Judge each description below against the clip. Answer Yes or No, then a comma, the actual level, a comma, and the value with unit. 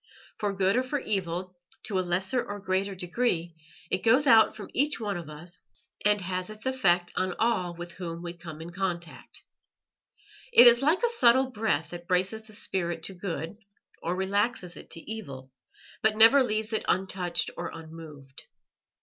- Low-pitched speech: No, high, 190 Hz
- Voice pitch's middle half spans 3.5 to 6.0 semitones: Yes, average, 4.2 semitones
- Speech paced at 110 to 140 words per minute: No, average, 175 wpm